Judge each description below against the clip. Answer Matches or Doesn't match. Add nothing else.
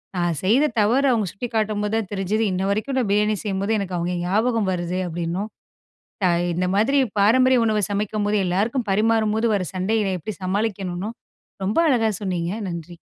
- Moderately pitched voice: Doesn't match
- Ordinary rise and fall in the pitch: Matches